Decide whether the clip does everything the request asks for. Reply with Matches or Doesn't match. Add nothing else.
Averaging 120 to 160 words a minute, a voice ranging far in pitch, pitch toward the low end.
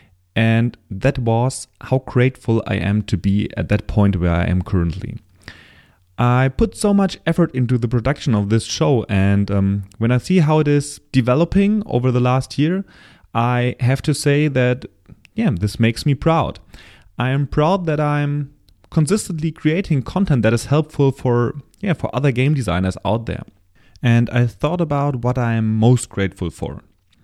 Doesn't match